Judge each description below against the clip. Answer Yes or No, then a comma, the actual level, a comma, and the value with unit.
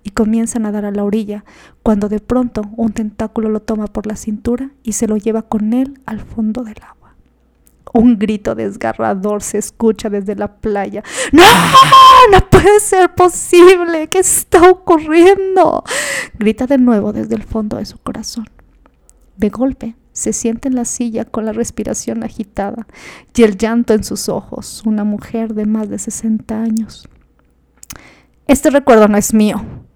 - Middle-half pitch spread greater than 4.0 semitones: No, average, 3.3 semitones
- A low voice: No, high, 225 Hz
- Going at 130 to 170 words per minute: Yes, average, 160 wpm